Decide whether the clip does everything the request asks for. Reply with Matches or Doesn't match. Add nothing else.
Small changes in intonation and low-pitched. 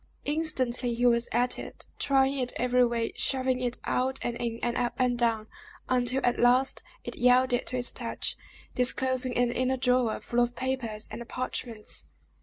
Doesn't match